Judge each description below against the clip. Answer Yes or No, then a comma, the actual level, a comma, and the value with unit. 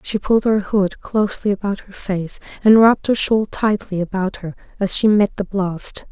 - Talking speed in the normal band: Yes, average, 195 wpm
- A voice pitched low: No, high, 200 Hz